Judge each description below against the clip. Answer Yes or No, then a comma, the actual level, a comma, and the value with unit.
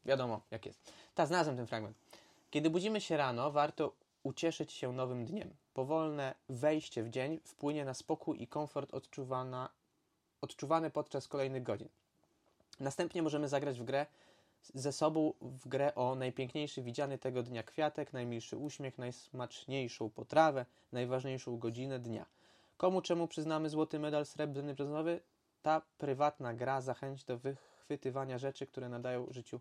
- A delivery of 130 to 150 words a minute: Yes, average, 140 wpm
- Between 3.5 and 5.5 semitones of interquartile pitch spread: No, average, 3.1 semitones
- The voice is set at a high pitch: No, low, 135 Hz